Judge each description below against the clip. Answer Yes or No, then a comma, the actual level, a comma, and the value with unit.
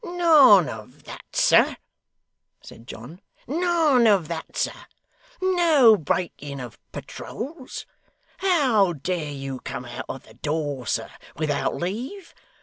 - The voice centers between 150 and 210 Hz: Yes, medium, 185 Hz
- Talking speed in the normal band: No, slow, 120 wpm